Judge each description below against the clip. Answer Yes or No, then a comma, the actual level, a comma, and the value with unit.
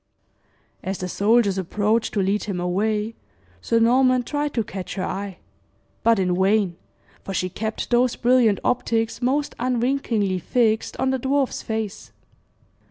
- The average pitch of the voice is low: No, high, 220 Hz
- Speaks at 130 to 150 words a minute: Yes, average, 145 wpm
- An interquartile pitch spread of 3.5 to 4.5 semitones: Yes, average, 4.1 semitones